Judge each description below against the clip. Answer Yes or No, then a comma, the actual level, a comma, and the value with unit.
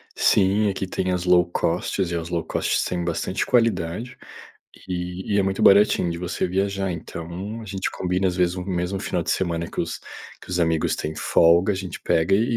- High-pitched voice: No, very low, 90 Hz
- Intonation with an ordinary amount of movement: No, narrow, 2.0 semitones